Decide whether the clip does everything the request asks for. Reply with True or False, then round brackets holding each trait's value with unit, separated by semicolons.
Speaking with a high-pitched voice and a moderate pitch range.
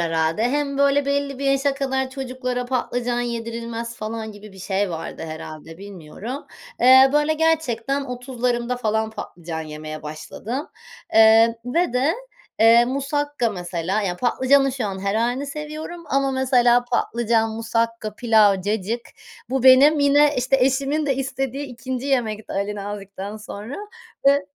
True (240 Hz; 4.2 semitones)